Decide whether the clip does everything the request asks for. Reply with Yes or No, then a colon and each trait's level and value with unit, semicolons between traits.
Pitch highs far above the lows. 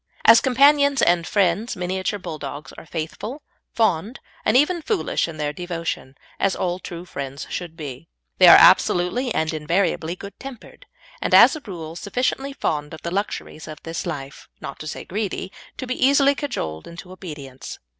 Yes: wide, 7.1 semitones